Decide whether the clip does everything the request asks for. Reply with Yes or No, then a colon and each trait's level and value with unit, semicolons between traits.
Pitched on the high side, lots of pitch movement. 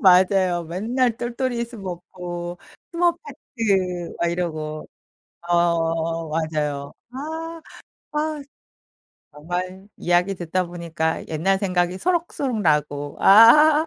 No: medium, 180 Hz; wide, 6.0 semitones